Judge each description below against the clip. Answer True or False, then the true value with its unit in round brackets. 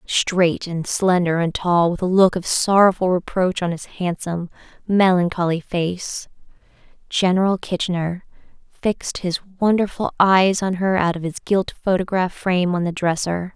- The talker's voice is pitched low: False (180 Hz)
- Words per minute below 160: True (145 wpm)